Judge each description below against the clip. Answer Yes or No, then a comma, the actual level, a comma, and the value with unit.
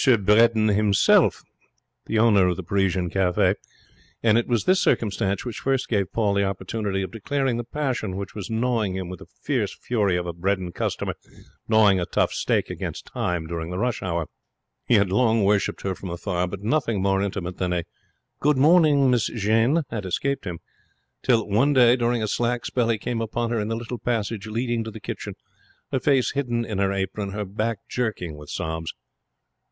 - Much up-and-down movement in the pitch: No, average, 3.7 semitones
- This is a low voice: Yes, low, 105 Hz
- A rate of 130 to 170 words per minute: No, average, 190 wpm